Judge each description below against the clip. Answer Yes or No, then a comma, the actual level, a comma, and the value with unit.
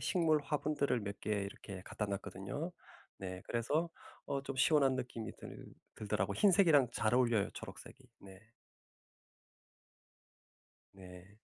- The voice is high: No, low, 120 Hz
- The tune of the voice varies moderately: No, wide, 6.6 semitones